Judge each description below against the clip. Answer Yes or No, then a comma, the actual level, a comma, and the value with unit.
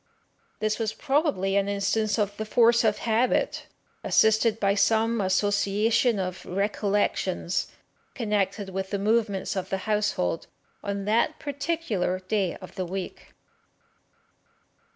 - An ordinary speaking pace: No, slow, 120 wpm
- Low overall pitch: No, high, 205 Hz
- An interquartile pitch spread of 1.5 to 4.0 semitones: Yes, narrow, 2.5 semitones